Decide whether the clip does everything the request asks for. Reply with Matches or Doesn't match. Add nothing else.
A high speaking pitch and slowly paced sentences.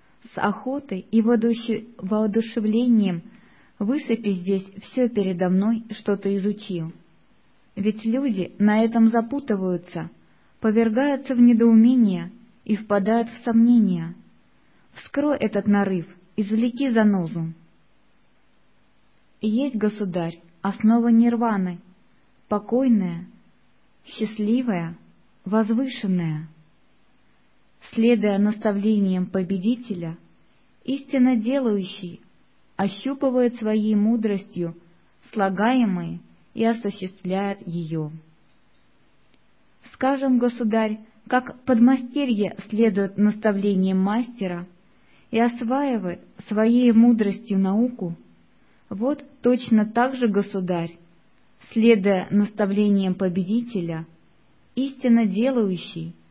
Matches